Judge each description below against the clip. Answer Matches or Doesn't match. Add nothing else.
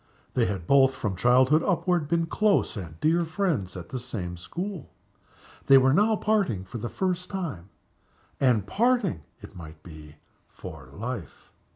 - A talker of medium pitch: Doesn't match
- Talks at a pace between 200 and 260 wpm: Doesn't match